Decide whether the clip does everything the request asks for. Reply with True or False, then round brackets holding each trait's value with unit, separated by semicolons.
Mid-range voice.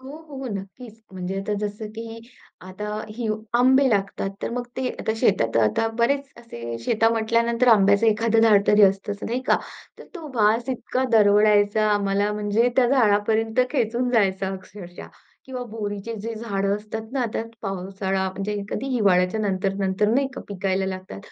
False (210 Hz)